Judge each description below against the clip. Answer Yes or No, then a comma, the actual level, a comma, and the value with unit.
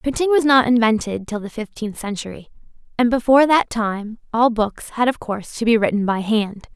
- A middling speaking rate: Yes, average, 195 wpm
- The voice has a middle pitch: No, high, 230 Hz